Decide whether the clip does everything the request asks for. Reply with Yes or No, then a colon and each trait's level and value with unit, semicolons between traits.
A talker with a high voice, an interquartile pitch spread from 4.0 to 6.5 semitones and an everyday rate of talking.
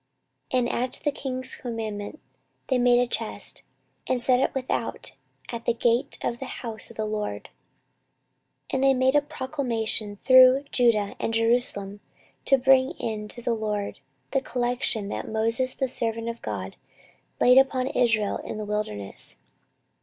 No: high, 240 Hz; average, 3.0 semitones; average, 160 wpm